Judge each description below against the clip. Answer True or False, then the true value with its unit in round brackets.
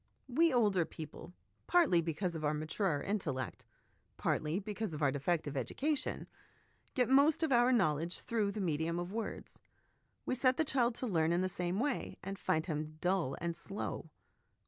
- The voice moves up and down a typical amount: False (7.1 semitones)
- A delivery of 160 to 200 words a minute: True (170 wpm)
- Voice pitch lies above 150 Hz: True (185 Hz)